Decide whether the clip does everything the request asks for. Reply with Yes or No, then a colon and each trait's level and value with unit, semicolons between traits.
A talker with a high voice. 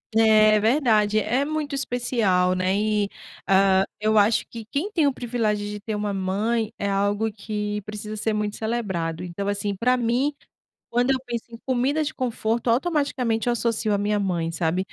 Yes: high, 215 Hz